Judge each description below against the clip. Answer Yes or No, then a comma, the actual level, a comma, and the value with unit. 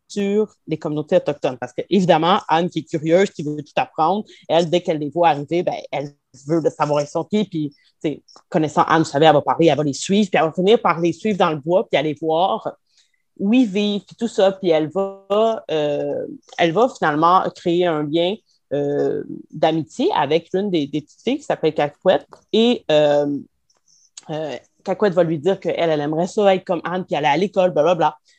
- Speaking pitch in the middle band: Yes, medium, 170 Hz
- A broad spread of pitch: No, average, 4.0 semitones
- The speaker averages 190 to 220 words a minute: Yes, average, 210 wpm